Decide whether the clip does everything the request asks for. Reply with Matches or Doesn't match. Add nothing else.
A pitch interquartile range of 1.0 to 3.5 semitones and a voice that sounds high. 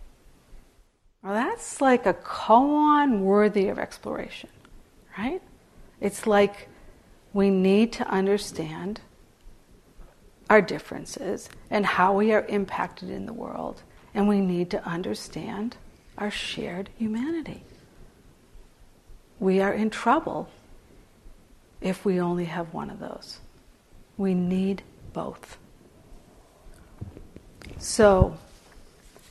Matches